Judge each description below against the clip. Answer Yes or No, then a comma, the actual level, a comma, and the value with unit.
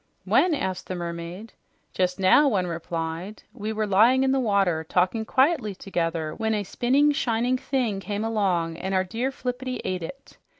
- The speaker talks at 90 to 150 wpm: No, average, 170 wpm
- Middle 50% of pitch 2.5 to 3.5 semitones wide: No, wide, 5.6 semitones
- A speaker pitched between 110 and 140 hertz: No, high, 205 Hz